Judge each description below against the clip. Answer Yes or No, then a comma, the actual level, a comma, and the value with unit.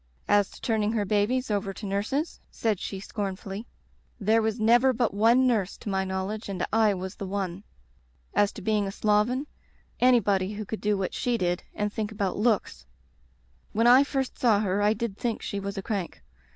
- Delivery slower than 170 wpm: No, average, 200 wpm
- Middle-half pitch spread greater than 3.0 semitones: No, narrow, 2.6 semitones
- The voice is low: No, high, 210 Hz